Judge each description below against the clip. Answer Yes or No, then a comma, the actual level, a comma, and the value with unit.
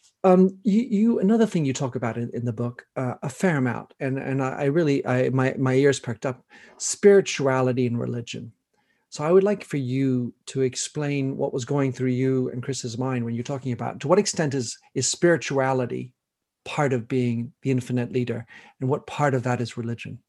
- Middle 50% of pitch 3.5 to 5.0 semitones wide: No, average, 2.9 semitones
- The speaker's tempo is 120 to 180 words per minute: No, fast, 205 wpm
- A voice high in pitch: No, low, 130 Hz